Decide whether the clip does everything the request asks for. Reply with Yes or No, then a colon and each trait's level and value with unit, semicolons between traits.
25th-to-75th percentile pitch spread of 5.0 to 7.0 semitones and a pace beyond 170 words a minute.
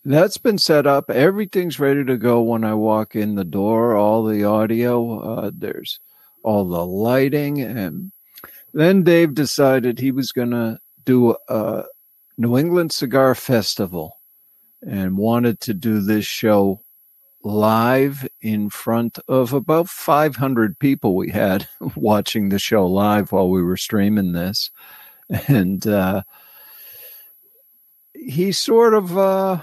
No: wide, 5.6 semitones; slow, 135 wpm